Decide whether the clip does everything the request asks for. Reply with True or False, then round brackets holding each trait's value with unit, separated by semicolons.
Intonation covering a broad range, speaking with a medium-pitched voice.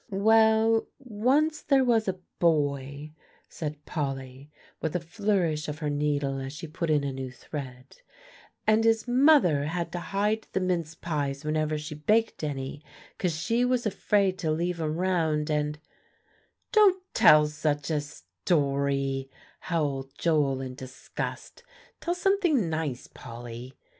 True (6.5 semitones; 155 Hz)